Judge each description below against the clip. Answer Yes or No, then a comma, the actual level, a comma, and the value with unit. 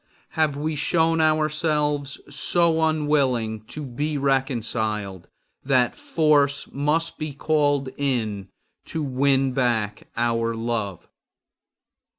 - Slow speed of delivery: Yes, slow, 100 wpm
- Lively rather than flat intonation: No, average, 4.5 semitones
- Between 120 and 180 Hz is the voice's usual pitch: Yes, medium, 140 Hz